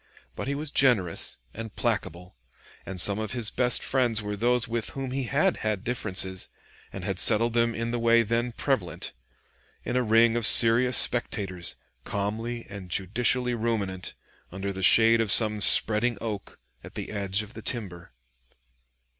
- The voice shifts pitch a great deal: No, average, 3.1 semitones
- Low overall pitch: Yes, low, 115 Hz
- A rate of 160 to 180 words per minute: Yes, average, 165 wpm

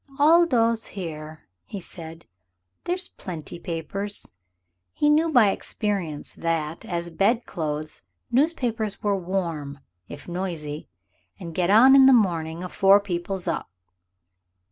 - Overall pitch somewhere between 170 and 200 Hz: Yes, medium, 185 Hz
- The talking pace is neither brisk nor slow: No, slow, 120 wpm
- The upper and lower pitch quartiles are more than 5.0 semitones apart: Yes, wide, 5.6 semitones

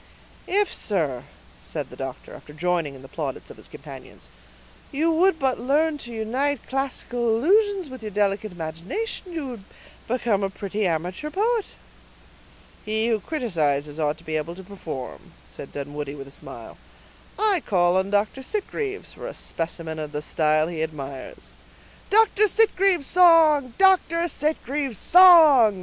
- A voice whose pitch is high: Yes, high, 220 Hz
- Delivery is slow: No, average, 150 wpm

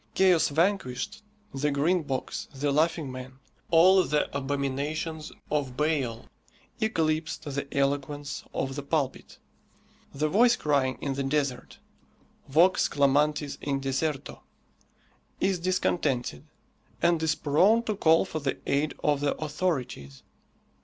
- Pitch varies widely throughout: No, average, 2.9 semitones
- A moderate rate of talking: No, slow, 120 wpm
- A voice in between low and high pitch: Yes, medium, 150 Hz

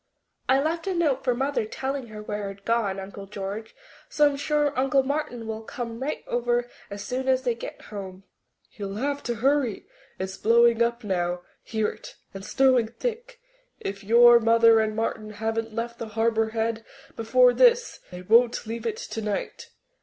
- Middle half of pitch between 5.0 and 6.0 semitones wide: No, average, 3.5 semitones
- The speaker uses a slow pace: No, average, 175 wpm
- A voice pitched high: Yes, high, 230 Hz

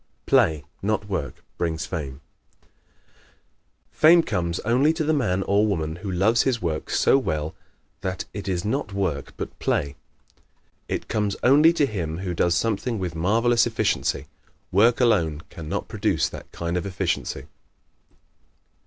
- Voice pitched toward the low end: Yes, very low, 95 Hz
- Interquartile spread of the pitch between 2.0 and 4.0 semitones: No, wide, 5.6 semitones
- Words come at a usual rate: Yes, average, 150 wpm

